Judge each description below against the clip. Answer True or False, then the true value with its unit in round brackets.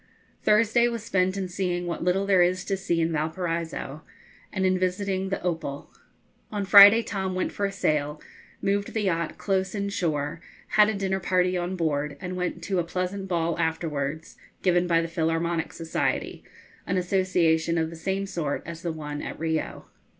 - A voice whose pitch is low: False (180 Hz)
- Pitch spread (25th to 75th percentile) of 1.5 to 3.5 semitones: True (2.8 semitones)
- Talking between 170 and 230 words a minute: True (175 wpm)